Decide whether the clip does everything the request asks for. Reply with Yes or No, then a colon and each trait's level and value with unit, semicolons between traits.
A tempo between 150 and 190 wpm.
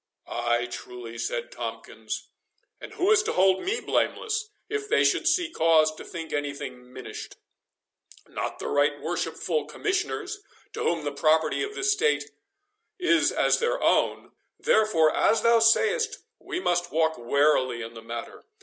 Yes: average, 155 wpm